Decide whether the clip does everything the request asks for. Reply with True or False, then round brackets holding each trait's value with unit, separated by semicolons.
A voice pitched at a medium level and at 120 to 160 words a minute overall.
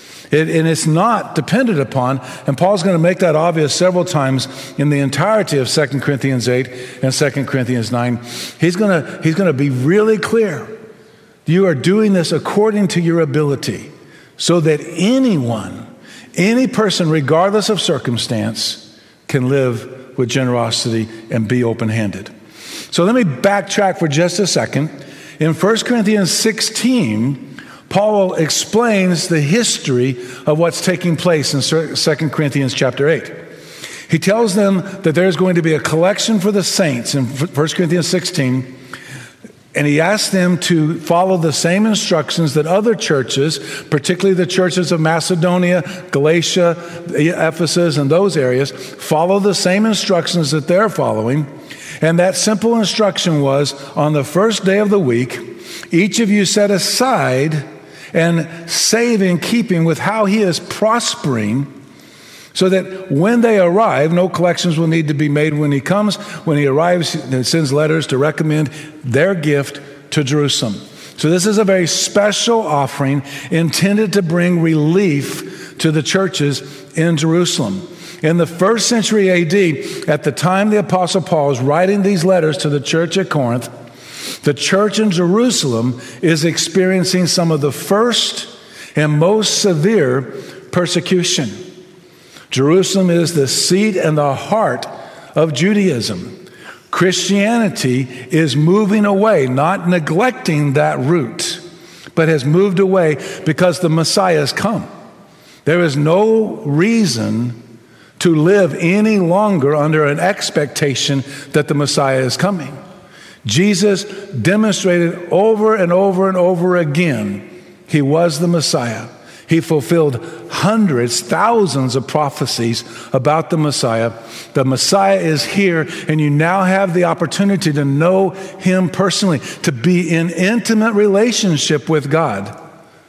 True (170 Hz; 140 wpm)